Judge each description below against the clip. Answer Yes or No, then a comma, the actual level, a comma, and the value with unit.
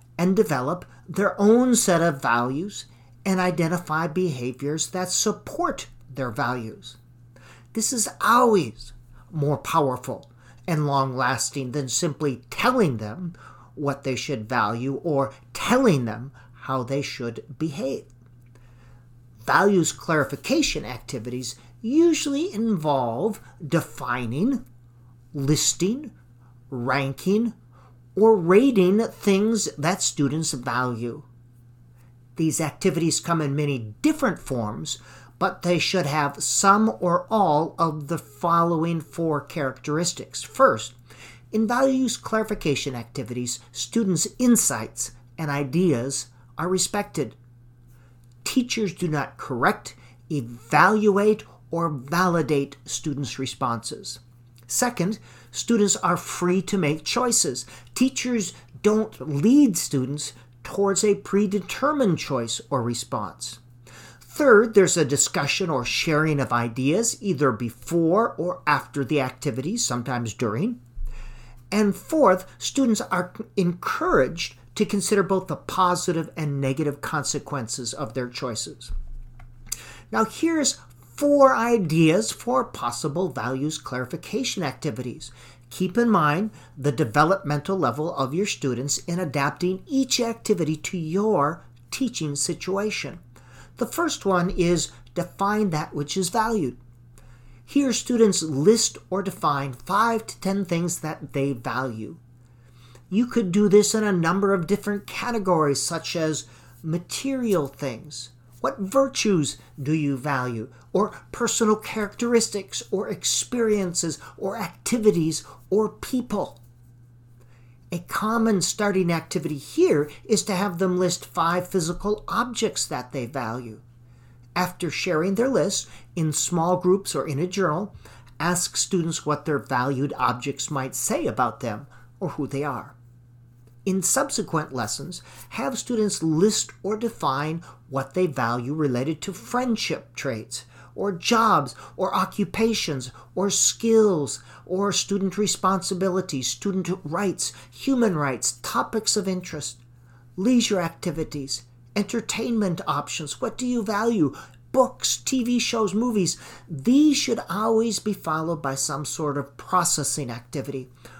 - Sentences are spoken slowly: Yes, slow, 115 wpm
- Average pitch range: No, wide, 8.0 semitones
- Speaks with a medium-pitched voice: Yes, medium, 155 Hz